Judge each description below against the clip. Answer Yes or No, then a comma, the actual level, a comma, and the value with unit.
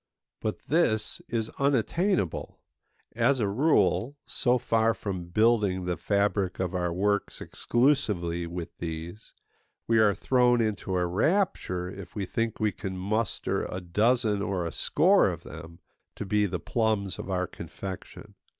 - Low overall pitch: Yes, low, 105 Hz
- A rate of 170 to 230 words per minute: No, average, 145 wpm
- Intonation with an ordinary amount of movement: Yes, average, 4.1 semitones